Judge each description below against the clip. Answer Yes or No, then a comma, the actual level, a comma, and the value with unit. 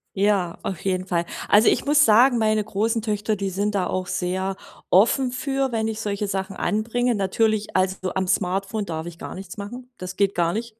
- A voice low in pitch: No, high, 205 Hz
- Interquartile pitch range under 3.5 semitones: Yes, average, 2.8 semitones